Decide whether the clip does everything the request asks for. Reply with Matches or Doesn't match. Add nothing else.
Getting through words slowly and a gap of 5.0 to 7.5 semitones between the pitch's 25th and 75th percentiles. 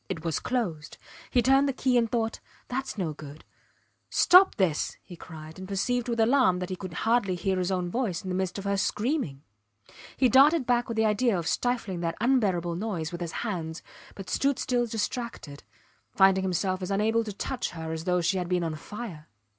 Doesn't match